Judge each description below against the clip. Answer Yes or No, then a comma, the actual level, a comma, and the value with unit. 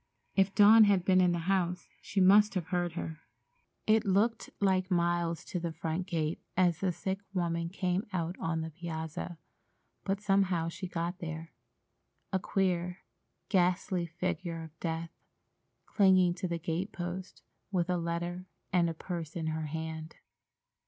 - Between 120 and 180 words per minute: Yes, average, 150 wpm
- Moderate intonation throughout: No, narrow, 2.1 semitones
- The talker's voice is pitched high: No, medium, 175 Hz